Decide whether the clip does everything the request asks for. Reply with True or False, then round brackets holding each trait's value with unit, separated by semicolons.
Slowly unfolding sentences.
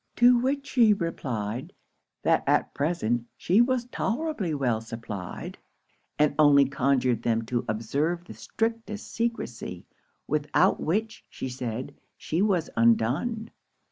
True (120 wpm)